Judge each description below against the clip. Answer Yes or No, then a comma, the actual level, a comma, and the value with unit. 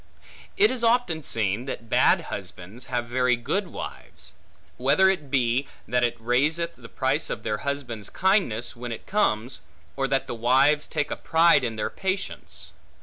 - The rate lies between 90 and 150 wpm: No, average, 165 wpm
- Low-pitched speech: Yes, low, 130 Hz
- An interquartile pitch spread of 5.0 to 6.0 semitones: Yes, wide, 5.6 semitones